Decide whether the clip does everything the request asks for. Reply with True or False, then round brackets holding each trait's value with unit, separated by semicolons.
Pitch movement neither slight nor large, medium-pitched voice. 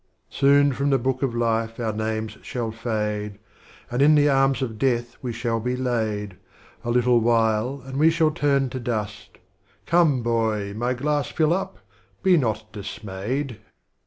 False (3.8 semitones; 120 Hz)